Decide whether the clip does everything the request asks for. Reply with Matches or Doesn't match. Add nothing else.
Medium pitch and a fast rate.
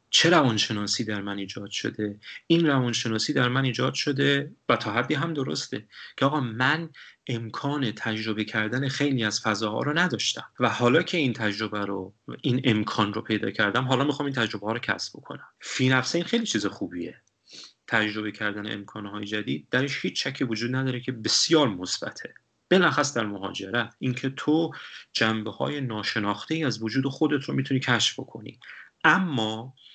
Doesn't match